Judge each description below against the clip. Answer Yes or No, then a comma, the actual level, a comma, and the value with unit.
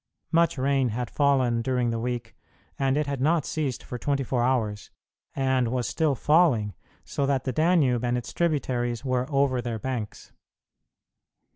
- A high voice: No, low, 130 Hz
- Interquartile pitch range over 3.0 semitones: No, narrow, 2.6 semitones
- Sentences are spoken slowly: No, average, 160 wpm